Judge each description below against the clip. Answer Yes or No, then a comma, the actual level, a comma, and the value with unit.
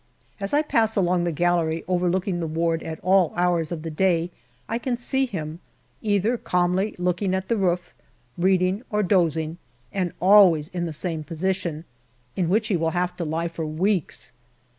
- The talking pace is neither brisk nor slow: Yes, average, 175 wpm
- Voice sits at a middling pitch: Yes, medium, 180 Hz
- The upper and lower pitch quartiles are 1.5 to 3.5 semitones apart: Yes, average, 2.8 semitones